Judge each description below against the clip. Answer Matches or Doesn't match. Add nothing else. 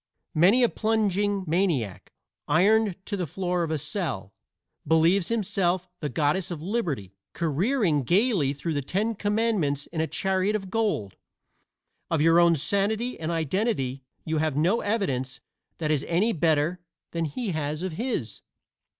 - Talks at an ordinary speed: Matches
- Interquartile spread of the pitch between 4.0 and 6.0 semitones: Matches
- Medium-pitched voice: Matches